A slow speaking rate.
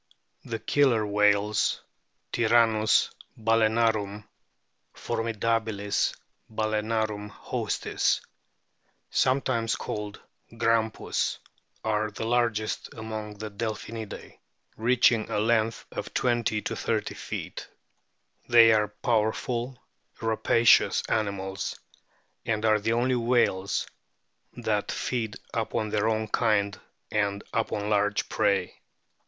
Yes: slow, 100 wpm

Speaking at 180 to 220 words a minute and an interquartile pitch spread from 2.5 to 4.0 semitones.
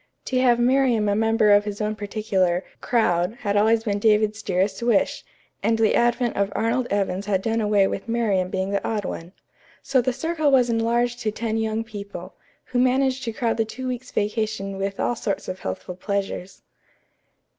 Yes: average, 185 wpm; average, 3.0 semitones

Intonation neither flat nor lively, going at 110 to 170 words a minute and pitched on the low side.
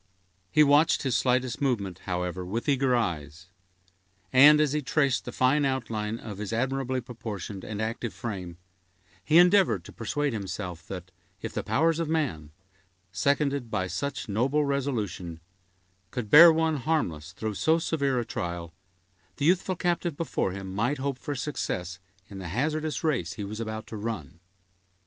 No: wide, 6.9 semitones; average, 160 wpm; low, 120 Hz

